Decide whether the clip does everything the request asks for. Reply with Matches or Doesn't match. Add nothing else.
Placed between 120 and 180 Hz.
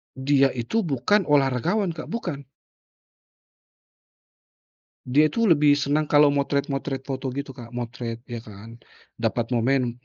Matches